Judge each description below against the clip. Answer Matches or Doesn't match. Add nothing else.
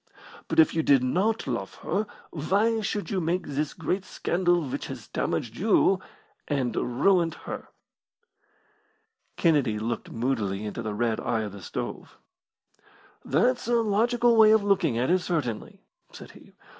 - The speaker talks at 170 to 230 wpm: Doesn't match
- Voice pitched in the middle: Matches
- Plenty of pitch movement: Matches